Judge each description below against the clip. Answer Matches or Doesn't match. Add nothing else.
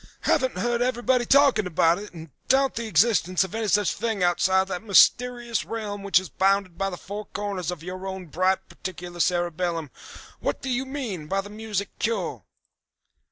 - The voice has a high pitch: Matches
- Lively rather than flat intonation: Doesn't match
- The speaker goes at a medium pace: Matches